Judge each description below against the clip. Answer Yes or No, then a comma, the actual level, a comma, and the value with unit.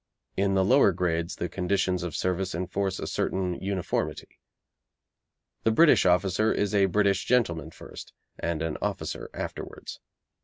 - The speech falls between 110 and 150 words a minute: Yes, average, 140 wpm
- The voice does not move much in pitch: Yes, narrow, 2.2 semitones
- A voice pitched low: Yes, very low, 95 Hz